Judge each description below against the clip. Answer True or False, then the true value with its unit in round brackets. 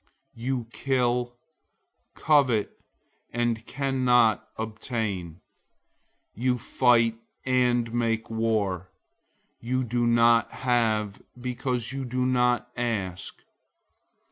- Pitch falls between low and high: False (120 Hz)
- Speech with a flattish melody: True (1.9 semitones)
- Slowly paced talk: True (75 wpm)